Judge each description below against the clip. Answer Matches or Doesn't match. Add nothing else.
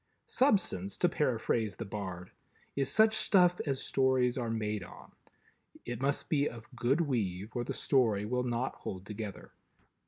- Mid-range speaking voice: Doesn't match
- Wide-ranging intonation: Doesn't match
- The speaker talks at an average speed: Matches